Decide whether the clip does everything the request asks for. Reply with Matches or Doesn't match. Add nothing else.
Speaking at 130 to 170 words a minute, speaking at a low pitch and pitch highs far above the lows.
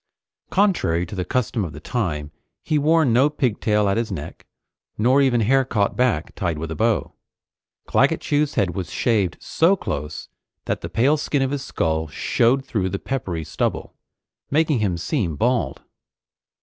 Matches